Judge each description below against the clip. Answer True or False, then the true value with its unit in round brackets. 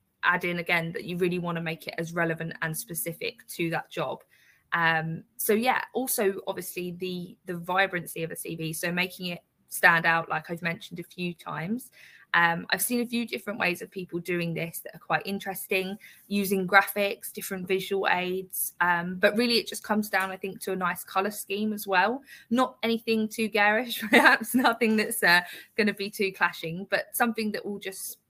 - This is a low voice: False (190 Hz)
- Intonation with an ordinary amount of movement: True (3.6 semitones)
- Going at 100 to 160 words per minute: False (195 wpm)